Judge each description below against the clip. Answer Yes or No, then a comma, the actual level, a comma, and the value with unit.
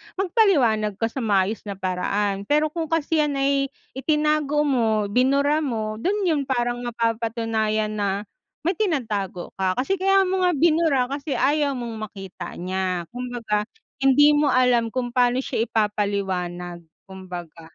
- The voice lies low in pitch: No, high, 240 Hz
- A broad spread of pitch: Yes, wide, 6.1 semitones